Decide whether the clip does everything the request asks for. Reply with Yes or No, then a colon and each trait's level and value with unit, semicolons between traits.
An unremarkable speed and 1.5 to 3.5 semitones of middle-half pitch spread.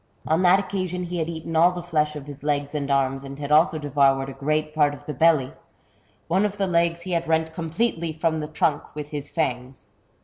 No: fast, 225 wpm; average, 2.8 semitones